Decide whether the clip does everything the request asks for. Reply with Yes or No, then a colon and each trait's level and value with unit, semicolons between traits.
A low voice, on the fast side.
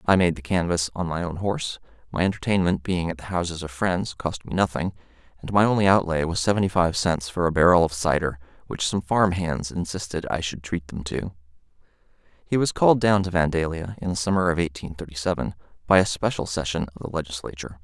Yes: very low, 85 Hz; fast, 210 wpm